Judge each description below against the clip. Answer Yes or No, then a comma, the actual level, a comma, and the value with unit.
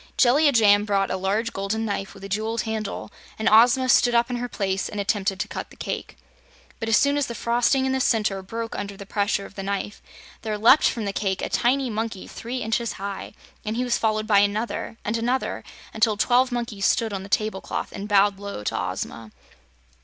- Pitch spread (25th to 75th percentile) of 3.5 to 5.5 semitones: No, average, 2.9 semitones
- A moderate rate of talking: No, fast, 215 wpm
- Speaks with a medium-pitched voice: No, high, 215 Hz